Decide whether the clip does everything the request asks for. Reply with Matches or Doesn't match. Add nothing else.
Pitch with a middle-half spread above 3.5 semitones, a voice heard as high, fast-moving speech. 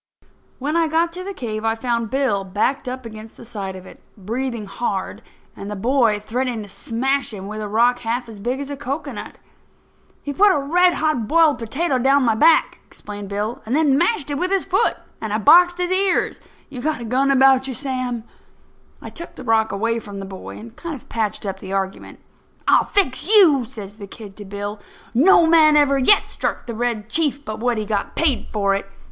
Matches